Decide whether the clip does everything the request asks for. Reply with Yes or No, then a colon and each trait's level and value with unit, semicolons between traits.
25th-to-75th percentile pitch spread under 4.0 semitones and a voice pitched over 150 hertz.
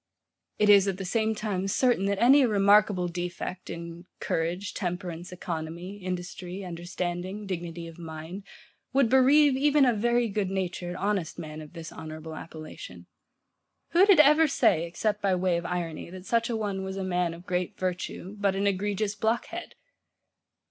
Yes: average, 3.3 semitones; medium, 185 Hz